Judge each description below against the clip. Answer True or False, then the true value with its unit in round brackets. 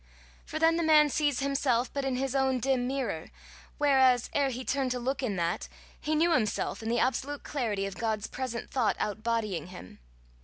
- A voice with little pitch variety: False (3.7 semitones)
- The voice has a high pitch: True (255 Hz)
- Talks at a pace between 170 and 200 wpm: True (195 wpm)